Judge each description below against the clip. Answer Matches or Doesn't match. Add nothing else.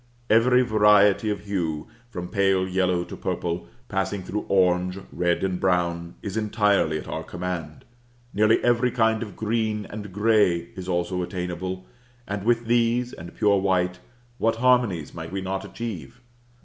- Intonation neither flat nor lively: Matches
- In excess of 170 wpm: Doesn't match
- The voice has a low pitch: Matches